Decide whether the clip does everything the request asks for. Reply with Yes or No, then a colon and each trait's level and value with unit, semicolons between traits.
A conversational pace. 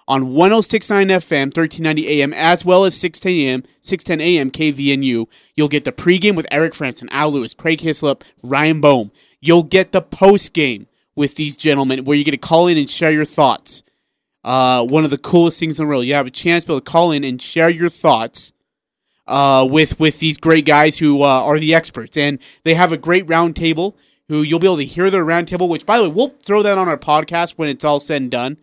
No: fast, 225 wpm